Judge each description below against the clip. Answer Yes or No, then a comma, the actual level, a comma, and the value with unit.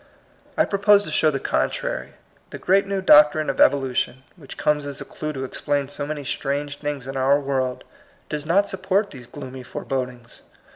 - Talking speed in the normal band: Yes, average, 180 wpm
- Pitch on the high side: No, medium, 145 Hz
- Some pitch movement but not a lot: Yes, average, 3.0 semitones